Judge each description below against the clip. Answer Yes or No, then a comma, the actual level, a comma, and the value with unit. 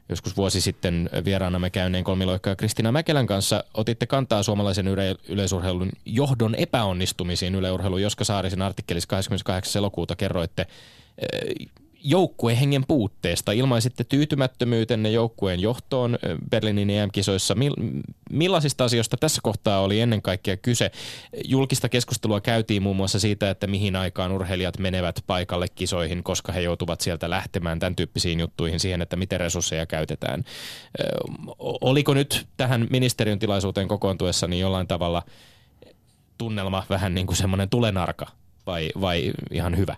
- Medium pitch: No, low, 100 Hz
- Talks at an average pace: Yes, average, 130 wpm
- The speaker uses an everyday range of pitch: Yes, average, 4.0 semitones